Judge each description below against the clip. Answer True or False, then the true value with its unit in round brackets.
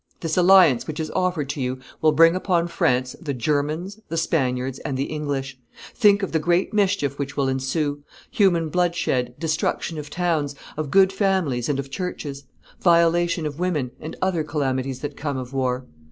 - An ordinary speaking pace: True (175 wpm)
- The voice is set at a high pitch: False (155 Hz)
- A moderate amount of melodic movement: True (4.2 semitones)